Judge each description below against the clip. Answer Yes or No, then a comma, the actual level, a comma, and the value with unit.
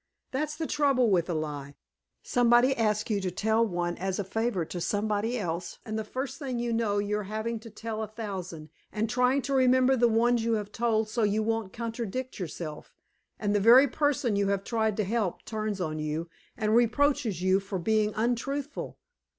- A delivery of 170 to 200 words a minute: Yes, average, 195 wpm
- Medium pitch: No, high, 220 Hz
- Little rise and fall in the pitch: No, average, 3.4 semitones